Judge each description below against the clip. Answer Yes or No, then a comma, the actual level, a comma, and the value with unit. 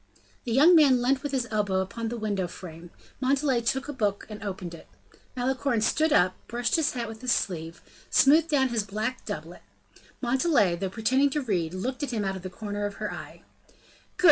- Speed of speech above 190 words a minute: Yes, average, 200 wpm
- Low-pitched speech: No, high, 230 Hz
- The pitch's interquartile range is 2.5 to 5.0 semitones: No, wide, 5.4 semitones